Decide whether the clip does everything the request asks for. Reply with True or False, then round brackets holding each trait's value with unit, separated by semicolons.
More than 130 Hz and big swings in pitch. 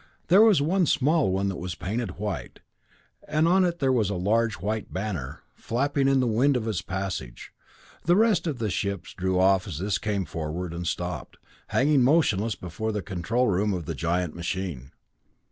False (105 Hz; 6.8 semitones)